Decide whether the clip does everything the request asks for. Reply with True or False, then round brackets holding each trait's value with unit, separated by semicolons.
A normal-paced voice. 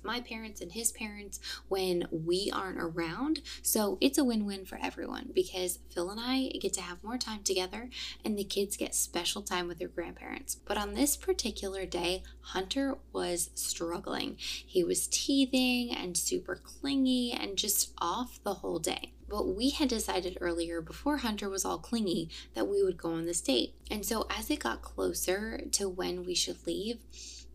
True (180 wpm)